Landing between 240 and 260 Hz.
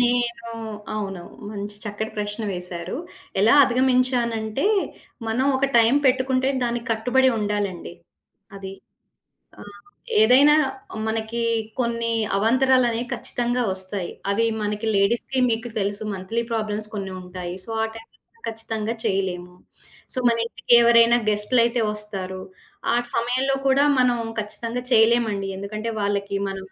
No: high, 225 Hz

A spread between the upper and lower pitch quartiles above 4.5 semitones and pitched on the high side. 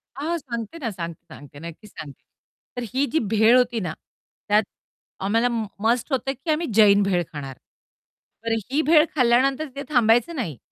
Yes: wide, 5.4 semitones; high, 235 Hz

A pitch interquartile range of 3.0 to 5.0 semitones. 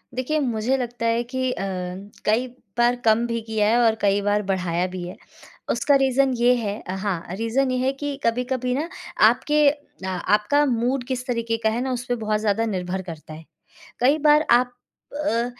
Yes: average, 3.7 semitones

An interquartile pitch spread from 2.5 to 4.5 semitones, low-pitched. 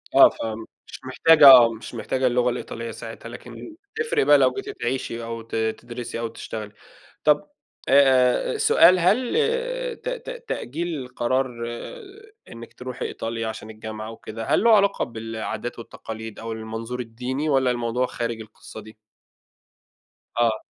Yes: average, 2.9 semitones; low, 120 Hz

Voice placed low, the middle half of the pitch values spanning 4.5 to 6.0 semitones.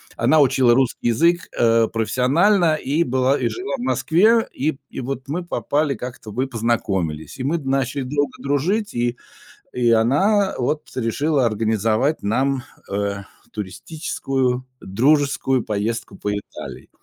Yes: low, 130 Hz; average, 4.9 semitones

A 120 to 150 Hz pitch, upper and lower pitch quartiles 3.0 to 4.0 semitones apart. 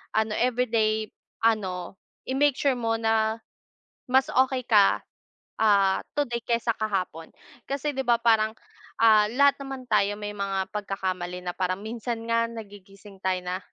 No: high, 220 Hz; average, 3.4 semitones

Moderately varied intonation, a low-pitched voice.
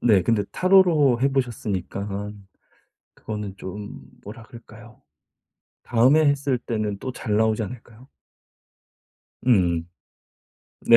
Yes: average, 3.8 semitones; low, 110 Hz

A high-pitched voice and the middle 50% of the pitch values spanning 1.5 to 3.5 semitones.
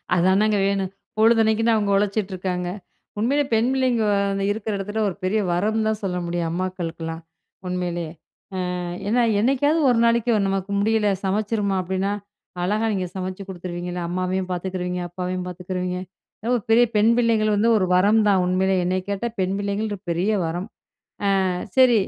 Yes: high, 195 Hz; average, 3.1 semitones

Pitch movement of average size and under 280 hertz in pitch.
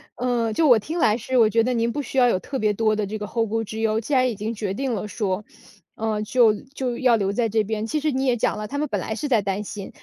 Yes: average, 3.0 semitones; high, 225 Hz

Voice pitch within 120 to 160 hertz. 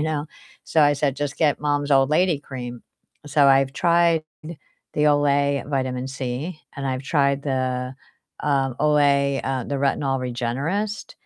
Yes: medium, 140 Hz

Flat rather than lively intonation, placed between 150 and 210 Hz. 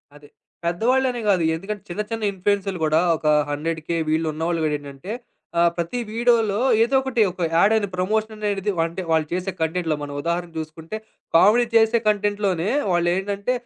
No: average, 4.5 semitones; medium, 185 Hz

